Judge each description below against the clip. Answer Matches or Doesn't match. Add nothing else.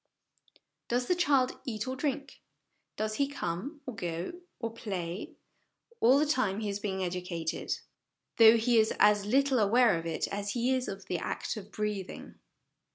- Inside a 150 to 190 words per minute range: Matches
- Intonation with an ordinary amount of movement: Matches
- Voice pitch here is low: Doesn't match